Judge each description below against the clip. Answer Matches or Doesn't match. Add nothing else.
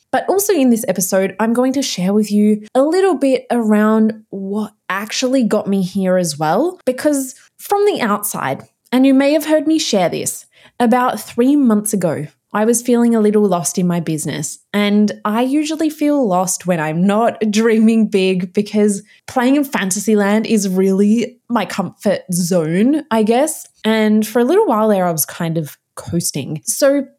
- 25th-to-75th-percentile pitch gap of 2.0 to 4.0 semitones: Doesn't match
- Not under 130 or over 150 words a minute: Doesn't match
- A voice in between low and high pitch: Doesn't match